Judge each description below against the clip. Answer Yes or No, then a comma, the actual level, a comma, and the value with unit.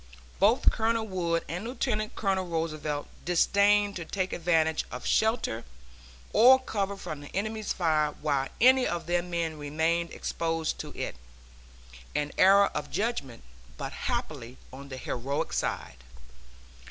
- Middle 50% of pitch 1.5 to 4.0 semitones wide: No, average, 5.2 semitones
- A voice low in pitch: No, medium, 170 Hz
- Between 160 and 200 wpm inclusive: No, slow, 135 wpm